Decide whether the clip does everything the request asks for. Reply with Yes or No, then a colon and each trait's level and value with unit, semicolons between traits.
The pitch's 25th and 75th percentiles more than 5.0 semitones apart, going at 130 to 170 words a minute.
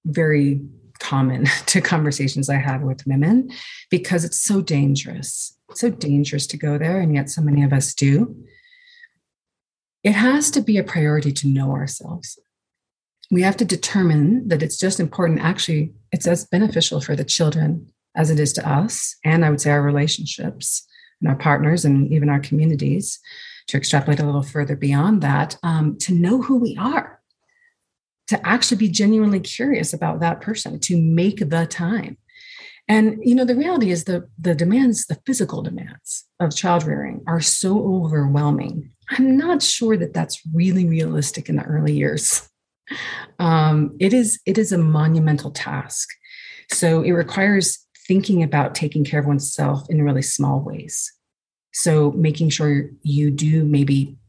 Yes: wide, 5.4 semitones; average, 165 wpm